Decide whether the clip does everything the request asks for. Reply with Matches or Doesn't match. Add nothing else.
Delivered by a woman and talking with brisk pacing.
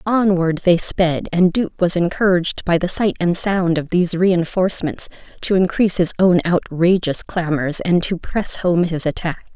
Doesn't match